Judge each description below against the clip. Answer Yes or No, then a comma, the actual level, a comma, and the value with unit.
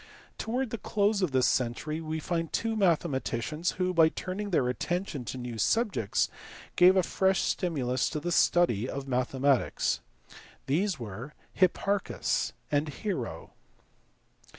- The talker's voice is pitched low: No, medium, 160 Hz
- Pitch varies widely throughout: Yes, wide, 6.3 semitones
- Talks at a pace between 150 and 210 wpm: No, slow, 135 wpm